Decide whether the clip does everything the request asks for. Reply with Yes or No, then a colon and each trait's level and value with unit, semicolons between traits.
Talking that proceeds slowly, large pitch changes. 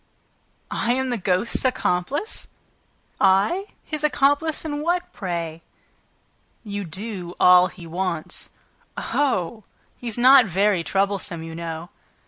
Yes: slow, 110 wpm; wide, 6.8 semitones